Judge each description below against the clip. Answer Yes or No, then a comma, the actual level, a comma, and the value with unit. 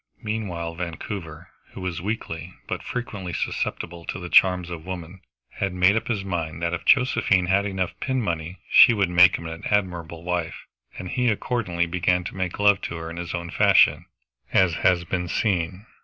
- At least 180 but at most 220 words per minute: Yes, average, 185 wpm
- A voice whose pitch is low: Yes, very low, 90 Hz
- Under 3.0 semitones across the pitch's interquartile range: Yes, narrow, 2.5 semitones